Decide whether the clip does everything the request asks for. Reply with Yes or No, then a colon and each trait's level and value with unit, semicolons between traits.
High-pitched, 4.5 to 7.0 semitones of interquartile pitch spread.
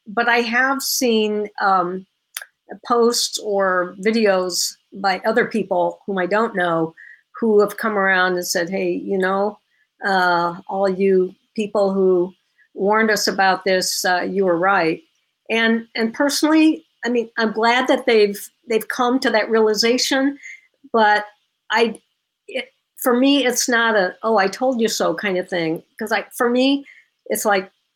No: high, 215 Hz; average, 3.8 semitones